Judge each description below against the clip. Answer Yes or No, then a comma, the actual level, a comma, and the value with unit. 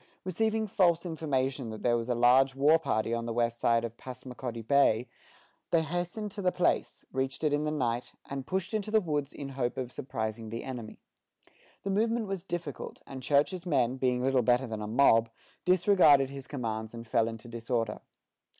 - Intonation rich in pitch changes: Yes, wide, 5.8 semitones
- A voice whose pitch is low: Yes, low, 130 Hz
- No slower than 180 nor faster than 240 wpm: Yes, average, 185 wpm